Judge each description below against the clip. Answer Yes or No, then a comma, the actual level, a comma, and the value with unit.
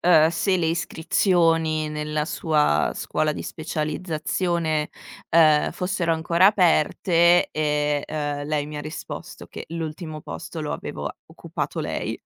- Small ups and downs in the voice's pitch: Yes, narrow, 1.9 semitones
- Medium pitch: Yes, medium, 160 Hz